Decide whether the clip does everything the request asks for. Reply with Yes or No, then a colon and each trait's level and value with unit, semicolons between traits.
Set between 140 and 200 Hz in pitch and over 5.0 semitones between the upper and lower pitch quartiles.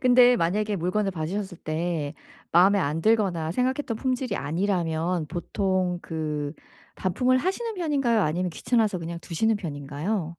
Yes: medium, 185 Hz; wide, 5.4 semitones